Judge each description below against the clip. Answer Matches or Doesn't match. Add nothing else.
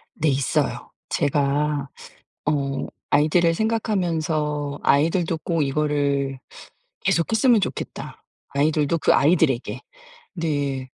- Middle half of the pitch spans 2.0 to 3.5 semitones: Matches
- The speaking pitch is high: Doesn't match